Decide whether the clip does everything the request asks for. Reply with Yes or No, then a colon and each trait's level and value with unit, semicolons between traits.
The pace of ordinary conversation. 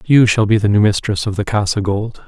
No: fast, 265 wpm